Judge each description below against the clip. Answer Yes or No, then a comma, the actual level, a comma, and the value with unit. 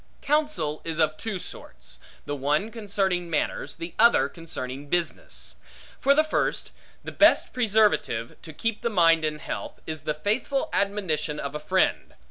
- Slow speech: No, average, 155 wpm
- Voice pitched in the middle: Yes, medium, 170 Hz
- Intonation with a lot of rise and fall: Yes, wide, 6.2 semitones